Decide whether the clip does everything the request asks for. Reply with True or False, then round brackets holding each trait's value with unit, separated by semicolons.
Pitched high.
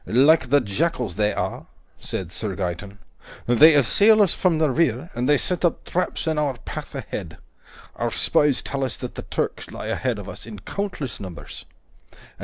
False (135 Hz)